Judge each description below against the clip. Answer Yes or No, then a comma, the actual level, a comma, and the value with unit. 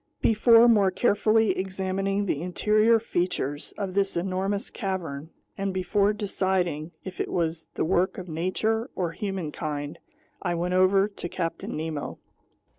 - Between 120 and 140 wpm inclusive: Yes, slow, 135 wpm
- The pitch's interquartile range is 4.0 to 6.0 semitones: No, average, 2.9 semitones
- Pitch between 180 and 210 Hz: Yes, medium, 185 Hz